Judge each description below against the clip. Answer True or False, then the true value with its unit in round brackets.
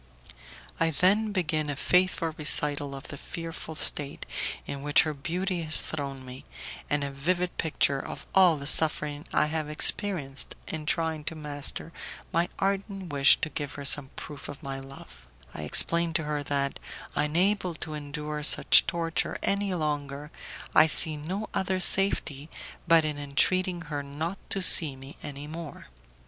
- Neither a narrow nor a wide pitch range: True (3.1 semitones)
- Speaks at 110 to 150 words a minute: False (160 wpm)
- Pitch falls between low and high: True (155 Hz)